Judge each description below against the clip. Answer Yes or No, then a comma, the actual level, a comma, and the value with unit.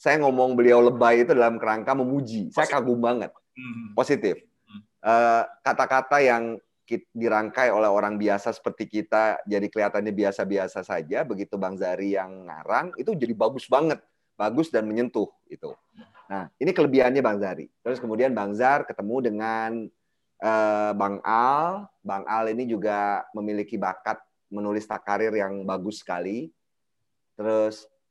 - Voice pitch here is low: Yes, low, 110 Hz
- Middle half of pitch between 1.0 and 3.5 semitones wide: Yes, average, 2.8 semitones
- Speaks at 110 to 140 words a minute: Yes, average, 130 wpm